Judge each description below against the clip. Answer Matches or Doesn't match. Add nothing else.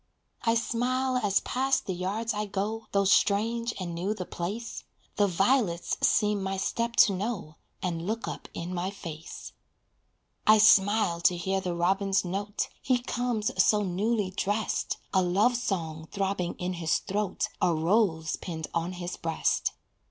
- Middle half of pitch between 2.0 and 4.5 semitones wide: Matches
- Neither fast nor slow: Matches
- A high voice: Matches